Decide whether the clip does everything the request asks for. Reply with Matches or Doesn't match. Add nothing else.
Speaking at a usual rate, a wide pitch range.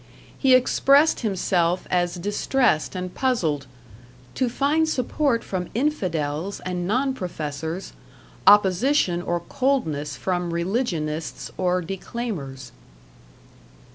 Doesn't match